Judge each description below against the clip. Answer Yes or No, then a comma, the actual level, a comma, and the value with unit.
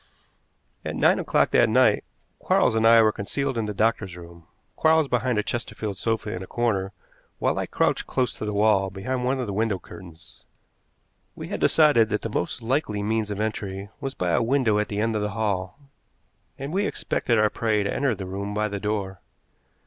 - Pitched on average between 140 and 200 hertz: No, low, 105 Hz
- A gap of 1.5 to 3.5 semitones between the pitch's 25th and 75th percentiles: Yes, average, 2.8 semitones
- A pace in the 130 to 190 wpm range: No, average, 200 wpm